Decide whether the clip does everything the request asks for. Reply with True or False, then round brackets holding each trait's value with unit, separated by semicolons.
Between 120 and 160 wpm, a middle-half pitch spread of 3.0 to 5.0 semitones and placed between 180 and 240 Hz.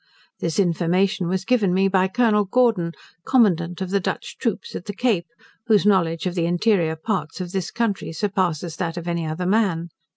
False (185 wpm; 3.3 semitones; 185 Hz)